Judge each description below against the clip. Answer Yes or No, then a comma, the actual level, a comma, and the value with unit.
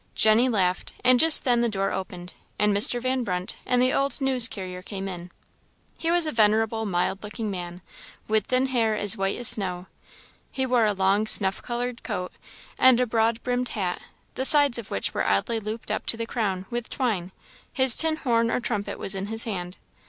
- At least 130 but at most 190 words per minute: No, average, 200 wpm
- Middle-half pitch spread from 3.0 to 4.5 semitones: Yes, average, 4.2 semitones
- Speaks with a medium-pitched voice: No, high, 220 Hz